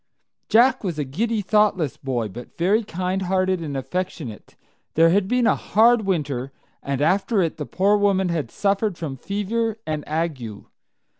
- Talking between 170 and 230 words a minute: No, average, 155 wpm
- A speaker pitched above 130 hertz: Yes, medium, 185 Hz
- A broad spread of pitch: Yes, wide, 5.7 semitones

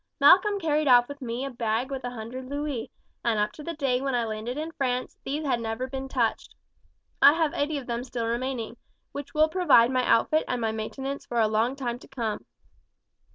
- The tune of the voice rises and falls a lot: No, average, 3.4 semitones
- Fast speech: Yes, fast, 210 wpm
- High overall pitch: Yes, very high, 255 Hz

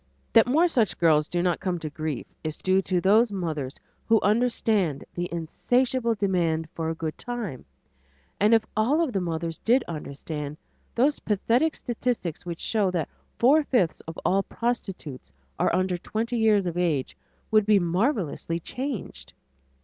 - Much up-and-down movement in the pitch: Yes, wide, 6.0 semitones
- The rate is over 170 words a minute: No, average, 155 wpm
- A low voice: No, high, 190 Hz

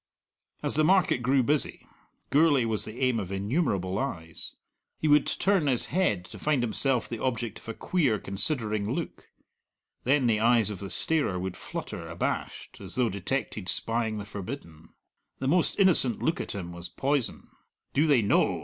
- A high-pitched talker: No, low, 120 Hz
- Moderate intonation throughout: No, wide, 6.0 semitones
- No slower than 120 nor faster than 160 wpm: No, average, 170 wpm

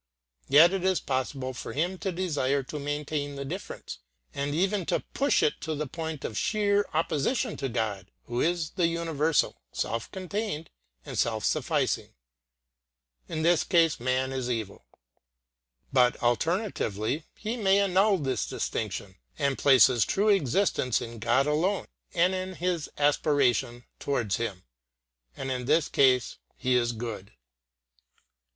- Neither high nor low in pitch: Yes, medium, 145 Hz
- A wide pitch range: Yes, wide, 5.9 semitones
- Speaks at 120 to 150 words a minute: Yes, average, 145 wpm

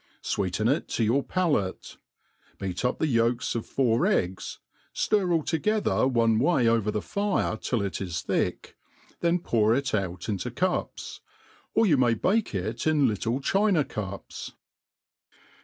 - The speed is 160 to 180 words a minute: No, average, 150 wpm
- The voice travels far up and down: Yes, wide, 7.3 semitones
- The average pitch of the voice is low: Yes, low, 120 Hz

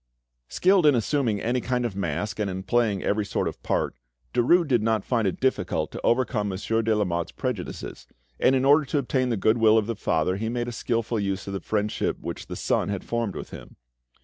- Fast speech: Yes, fast, 215 wpm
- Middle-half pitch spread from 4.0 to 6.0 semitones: No, average, 3.6 semitones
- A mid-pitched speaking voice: No, low, 110 Hz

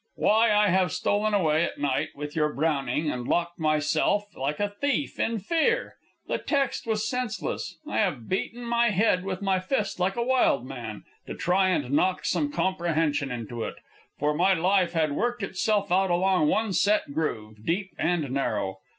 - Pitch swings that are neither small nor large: No, wide, 5.7 semitones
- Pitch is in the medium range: Yes, medium, 180 Hz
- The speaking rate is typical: Yes, average, 180 wpm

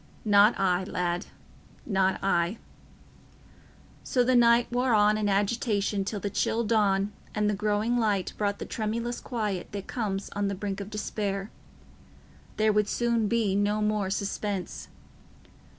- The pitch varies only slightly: Yes, narrow, 1.9 semitones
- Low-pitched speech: No, high, 210 Hz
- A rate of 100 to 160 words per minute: Yes, average, 140 wpm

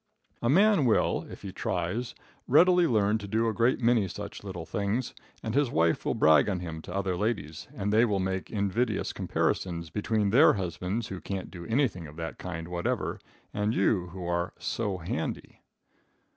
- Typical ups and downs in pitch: Yes, average, 4.5 semitones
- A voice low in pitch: Yes, low, 100 Hz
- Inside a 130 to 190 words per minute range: Yes, average, 180 wpm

